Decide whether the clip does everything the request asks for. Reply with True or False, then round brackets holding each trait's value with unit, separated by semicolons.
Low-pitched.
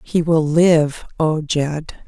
False (155 Hz)